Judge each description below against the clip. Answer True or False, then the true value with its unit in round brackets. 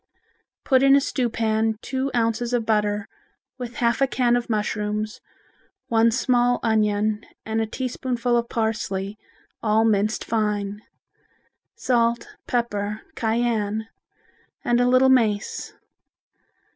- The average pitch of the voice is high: True (225 Hz)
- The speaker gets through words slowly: True (120 wpm)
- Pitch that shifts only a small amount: True (2.3 semitones)